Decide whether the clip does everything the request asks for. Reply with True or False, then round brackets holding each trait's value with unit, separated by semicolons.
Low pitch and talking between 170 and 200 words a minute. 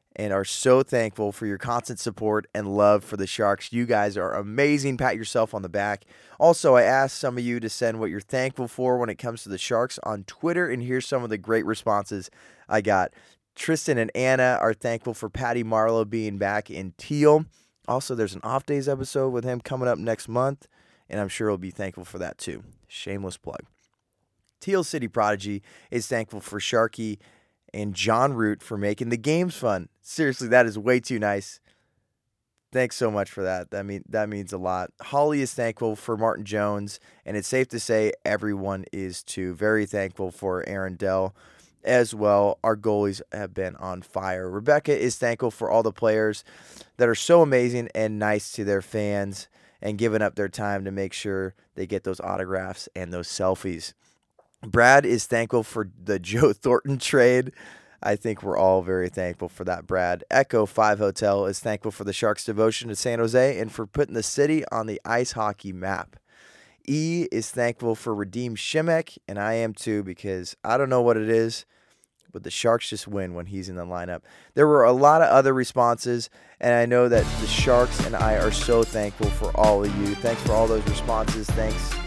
True (110 Hz; 195 wpm)